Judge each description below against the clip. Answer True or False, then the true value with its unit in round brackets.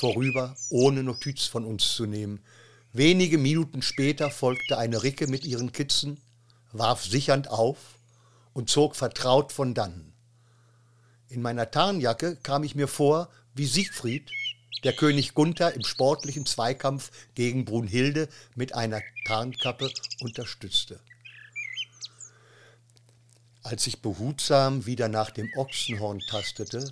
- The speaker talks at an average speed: False (120 wpm)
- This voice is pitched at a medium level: False (125 Hz)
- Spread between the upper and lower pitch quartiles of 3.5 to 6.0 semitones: False (2.8 semitones)